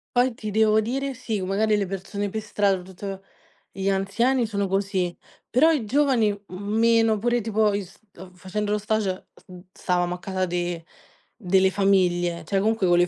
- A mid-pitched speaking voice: No, high, 200 Hz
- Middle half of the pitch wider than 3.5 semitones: No, average, 2.7 semitones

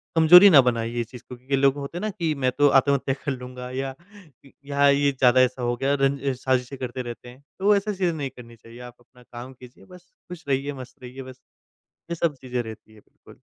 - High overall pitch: No, low, 130 Hz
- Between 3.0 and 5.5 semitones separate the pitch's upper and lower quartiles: No, narrow, 2.4 semitones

